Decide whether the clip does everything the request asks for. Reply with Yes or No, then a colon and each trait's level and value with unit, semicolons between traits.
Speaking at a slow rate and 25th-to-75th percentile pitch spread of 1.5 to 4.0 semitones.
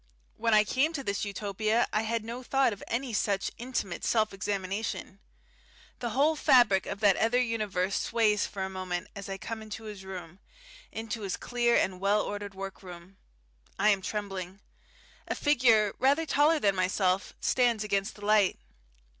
No: average, 165 wpm; average, 3.1 semitones